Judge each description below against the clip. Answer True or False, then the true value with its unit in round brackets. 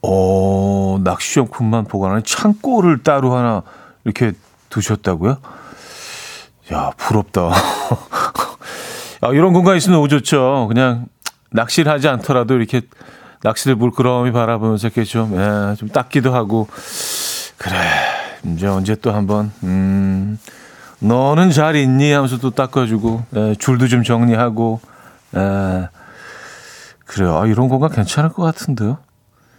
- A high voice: False (115 Hz)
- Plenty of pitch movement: False (4.1 semitones)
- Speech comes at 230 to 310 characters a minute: True (250 characters per minute)